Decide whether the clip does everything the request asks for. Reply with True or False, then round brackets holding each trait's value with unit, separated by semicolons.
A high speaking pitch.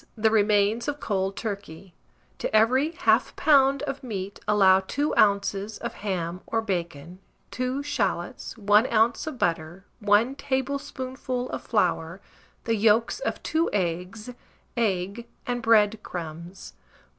True (210 Hz)